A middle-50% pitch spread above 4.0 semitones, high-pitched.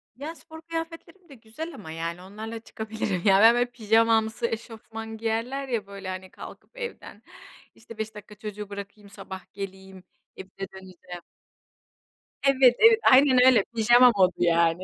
Yes: average, 4.4 semitones; high, 220 Hz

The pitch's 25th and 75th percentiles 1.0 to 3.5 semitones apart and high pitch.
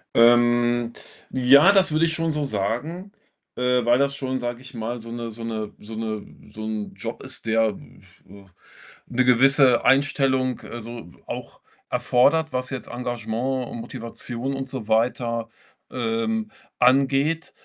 No: average, 2.8 semitones; low, 125 Hz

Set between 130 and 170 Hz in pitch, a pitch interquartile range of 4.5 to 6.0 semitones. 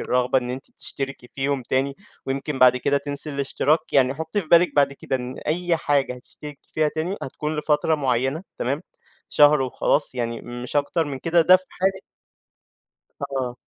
No: medium, 140 Hz; average, 3.1 semitones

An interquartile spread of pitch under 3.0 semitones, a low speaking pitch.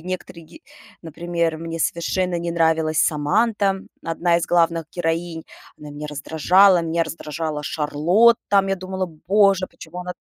No: narrow, 2.6 semitones; medium, 170 Hz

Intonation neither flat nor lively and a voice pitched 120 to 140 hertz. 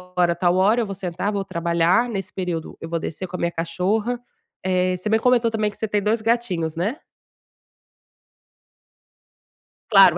No: average, 3.7 semitones; high, 190 Hz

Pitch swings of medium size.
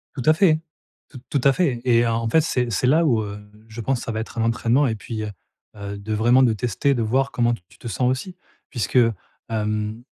Yes: average, 3.2 semitones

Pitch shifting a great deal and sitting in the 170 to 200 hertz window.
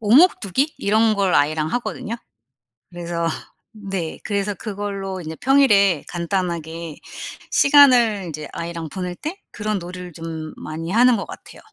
No: average, 4.3 semitones; high, 190 Hz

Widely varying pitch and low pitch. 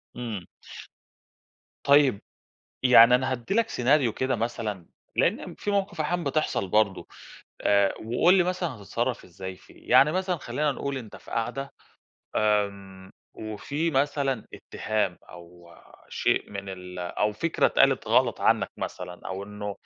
Yes: wide, 6.1 semitones; low, 115 Hz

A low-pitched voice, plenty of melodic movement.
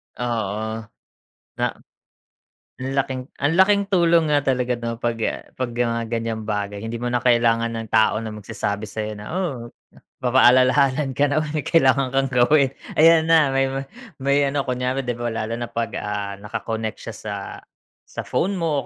No: low, 125 Hz; average, 3.7 semitones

